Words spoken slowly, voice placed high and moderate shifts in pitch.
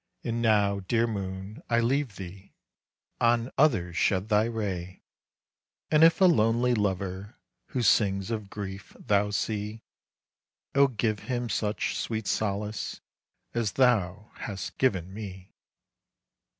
No: slow, 125 wpm; low, 105 Hz; average, 3.1 semitones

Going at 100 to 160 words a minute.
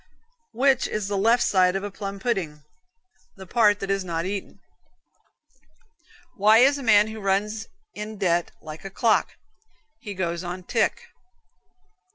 Yes: average, 150 wpm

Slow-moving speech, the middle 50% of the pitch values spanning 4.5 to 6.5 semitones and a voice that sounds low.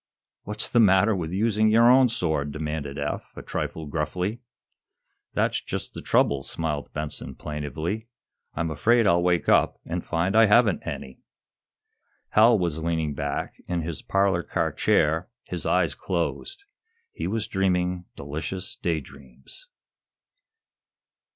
Yes: slow, 130 wpm; wide, 5.4 semitones; very low, 85 Hz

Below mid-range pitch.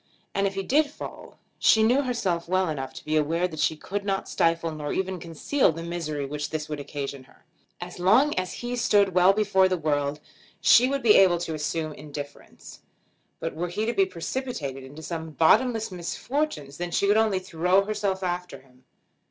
No: medium, 175 Hz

